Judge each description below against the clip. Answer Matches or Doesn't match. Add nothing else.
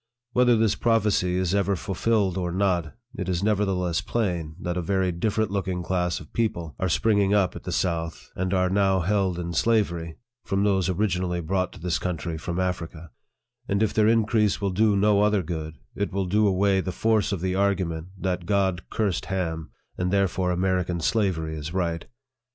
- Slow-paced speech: Doesn't match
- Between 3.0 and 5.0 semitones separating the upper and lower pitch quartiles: Doesn't match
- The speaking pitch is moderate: Doesn't match